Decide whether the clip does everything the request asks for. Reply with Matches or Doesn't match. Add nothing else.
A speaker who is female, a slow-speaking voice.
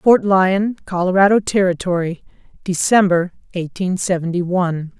Matches